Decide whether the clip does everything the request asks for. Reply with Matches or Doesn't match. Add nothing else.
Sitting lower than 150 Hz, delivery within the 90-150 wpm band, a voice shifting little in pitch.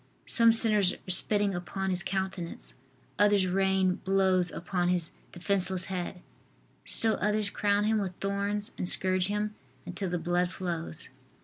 Doesn't match